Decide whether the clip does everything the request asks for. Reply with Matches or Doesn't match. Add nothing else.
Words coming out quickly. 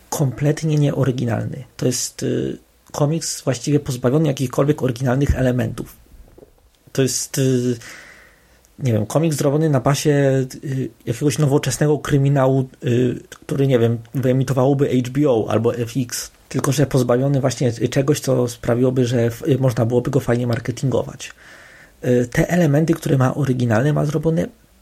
Doesn't match